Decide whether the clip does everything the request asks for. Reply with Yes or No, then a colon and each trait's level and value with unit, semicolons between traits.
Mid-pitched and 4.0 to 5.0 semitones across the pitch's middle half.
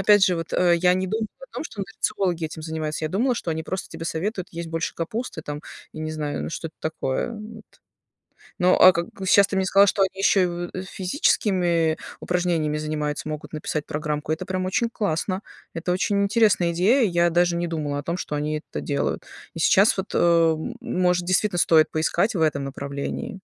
No: medium, 175 Hz; average, 3.5 semitones